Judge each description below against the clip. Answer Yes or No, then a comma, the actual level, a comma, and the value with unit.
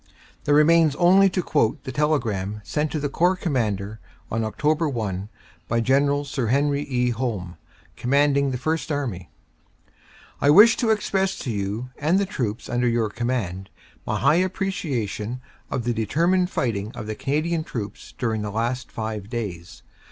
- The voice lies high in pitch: No, low, 130 Hz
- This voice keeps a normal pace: Yes, average, 160 wpm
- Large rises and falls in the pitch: Yes, wide, 5.9 semitones